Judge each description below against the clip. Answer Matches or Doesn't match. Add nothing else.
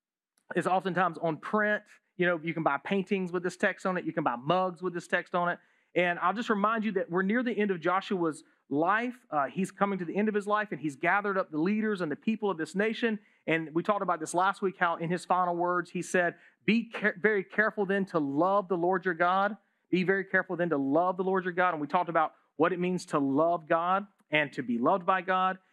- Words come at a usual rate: Doesn't match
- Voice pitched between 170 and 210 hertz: Matches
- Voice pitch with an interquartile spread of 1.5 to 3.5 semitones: Matches